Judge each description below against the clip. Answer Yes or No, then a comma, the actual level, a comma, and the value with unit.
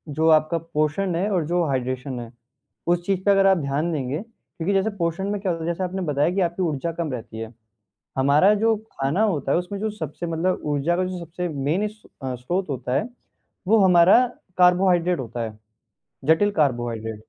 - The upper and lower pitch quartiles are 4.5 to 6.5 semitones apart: Yes, average, 5.0 semitones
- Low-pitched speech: No, medium, 170 Hz